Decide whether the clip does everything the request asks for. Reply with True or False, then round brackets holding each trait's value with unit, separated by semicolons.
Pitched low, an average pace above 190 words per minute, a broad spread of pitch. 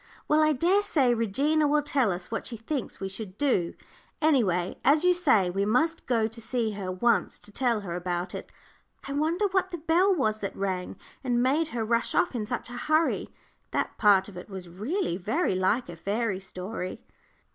False (230 Hz; 200 wpm; 7.7 semitones)